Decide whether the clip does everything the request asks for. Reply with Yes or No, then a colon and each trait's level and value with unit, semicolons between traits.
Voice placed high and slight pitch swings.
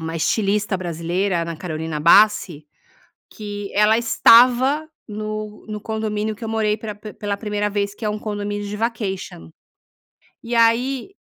Yes: high, 210 Hz; narrow, 1.9 semitones